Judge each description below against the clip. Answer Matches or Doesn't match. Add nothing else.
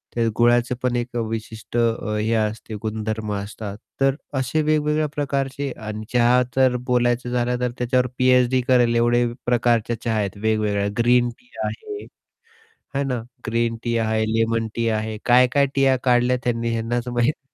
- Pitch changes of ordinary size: Doesn't match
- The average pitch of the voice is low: Matches